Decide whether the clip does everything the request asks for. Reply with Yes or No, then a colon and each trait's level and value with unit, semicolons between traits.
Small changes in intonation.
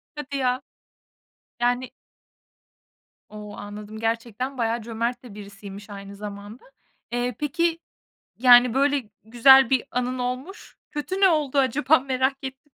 No: average, 3.6 semitones